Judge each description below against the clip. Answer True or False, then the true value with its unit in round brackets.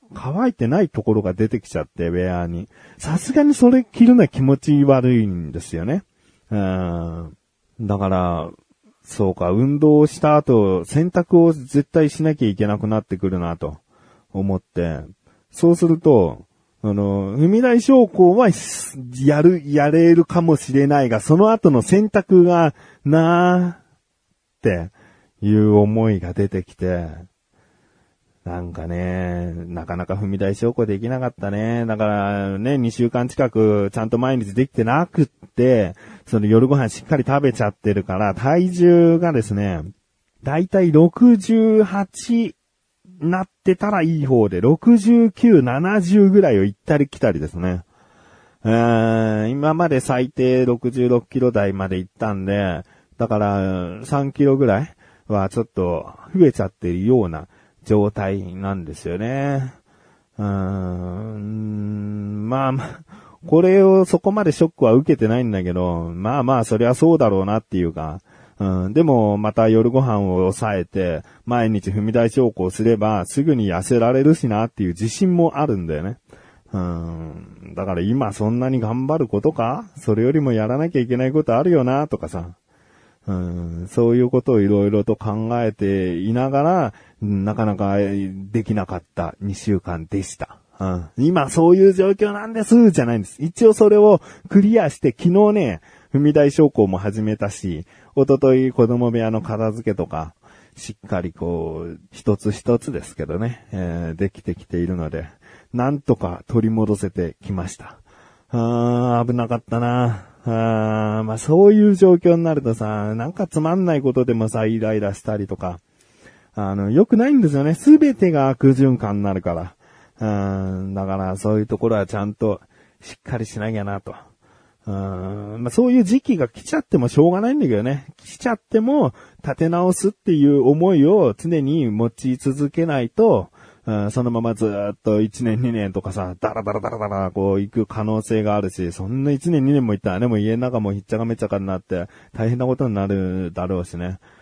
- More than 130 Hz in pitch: False (115 Hz)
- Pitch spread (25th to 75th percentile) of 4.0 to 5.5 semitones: False (6.8 semitones)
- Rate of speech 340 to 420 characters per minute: False (310 characters per minute)